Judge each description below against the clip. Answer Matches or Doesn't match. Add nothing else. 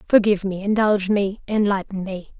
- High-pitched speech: Matches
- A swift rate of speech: Doesn't match